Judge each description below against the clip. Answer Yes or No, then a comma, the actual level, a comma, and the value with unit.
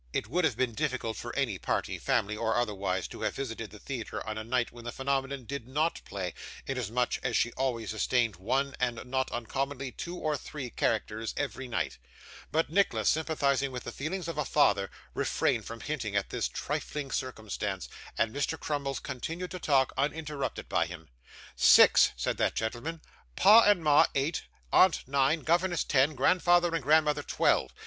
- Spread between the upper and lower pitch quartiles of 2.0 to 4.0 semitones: No, average, 4.8 semitones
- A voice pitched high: No, low, 135 Hz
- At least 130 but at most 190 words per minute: Yes, average, 175 wpm